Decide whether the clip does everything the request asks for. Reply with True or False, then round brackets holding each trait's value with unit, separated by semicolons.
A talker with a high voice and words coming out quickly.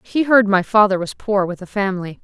True (200 Hz; 240 wpm)